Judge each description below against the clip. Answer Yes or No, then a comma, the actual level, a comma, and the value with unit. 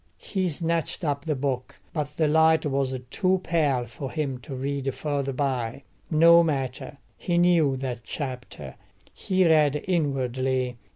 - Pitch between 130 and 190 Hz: Yes, medium, 140 Hz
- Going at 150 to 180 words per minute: No, average, 140 wpm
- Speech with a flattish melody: No, average, 3.7 semitones